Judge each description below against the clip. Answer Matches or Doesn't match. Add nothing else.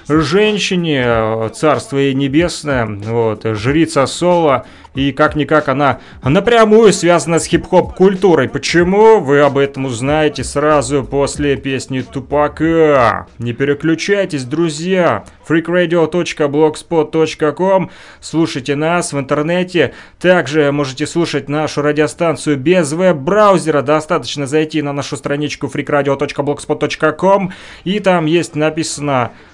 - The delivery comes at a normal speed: Doesn't match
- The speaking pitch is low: Doesn't match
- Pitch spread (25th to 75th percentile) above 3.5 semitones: Doesn't match